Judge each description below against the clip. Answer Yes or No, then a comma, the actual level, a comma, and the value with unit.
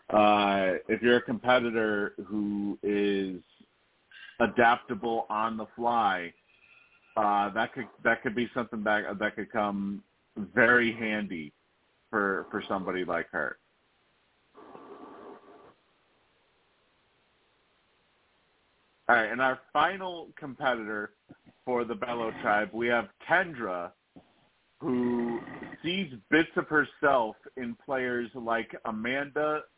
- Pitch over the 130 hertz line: No, low, 115 Hz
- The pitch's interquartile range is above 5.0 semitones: No, average, 3.4 semitones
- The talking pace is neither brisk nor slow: No, slow, 105 wpm